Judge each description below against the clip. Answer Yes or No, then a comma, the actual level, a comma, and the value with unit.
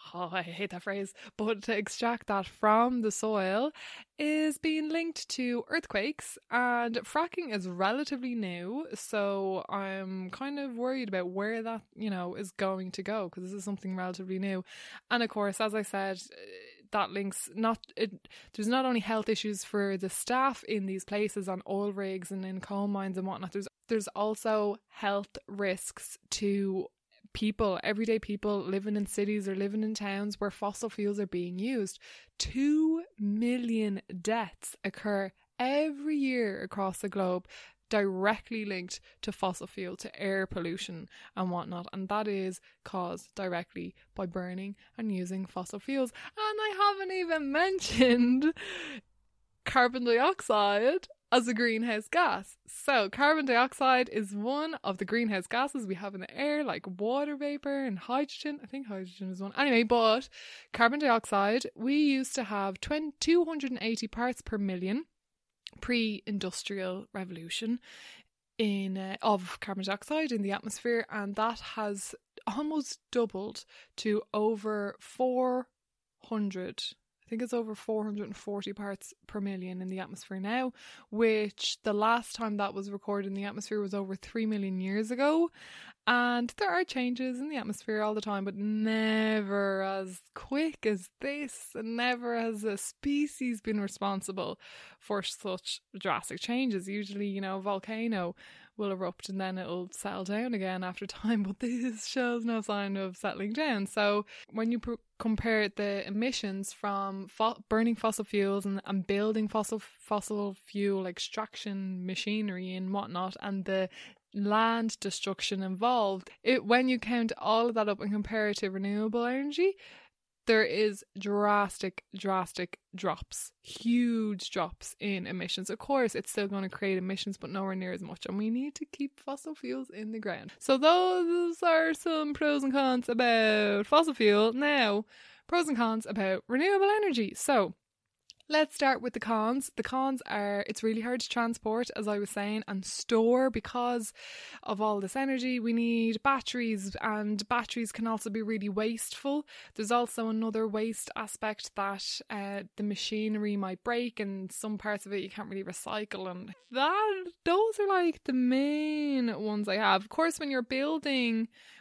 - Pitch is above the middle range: Yes, high, 215 Hz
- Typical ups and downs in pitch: Yes, average, 3.8 semitones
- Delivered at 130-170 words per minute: Yes, average, 160 wpm